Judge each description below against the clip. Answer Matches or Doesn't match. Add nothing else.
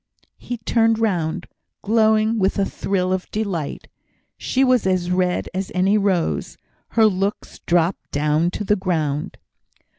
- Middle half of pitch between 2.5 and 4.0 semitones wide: Matches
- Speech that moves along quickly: Doesn't match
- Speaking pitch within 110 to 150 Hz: Doesn't match